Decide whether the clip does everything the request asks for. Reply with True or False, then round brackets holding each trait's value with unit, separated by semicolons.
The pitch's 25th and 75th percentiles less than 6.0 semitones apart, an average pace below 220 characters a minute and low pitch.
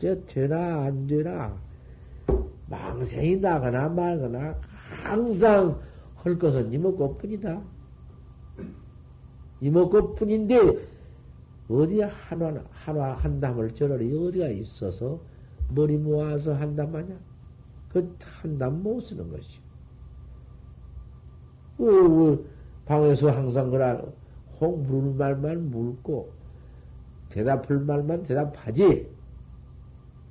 False (5.6 semitones; 175 characters per minute; 145 Hz)